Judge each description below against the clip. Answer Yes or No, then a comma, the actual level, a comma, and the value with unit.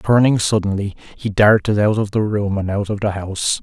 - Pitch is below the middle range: Yes, low, 105 Hz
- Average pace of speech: No, fast, 230 wpm